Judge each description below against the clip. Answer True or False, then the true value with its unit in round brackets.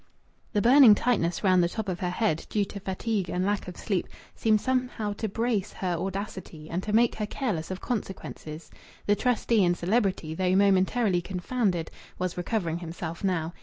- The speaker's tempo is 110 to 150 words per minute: False (175 wpm)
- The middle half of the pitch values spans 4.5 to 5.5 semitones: False (3.6 semitones)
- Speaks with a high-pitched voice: True (195 Hz)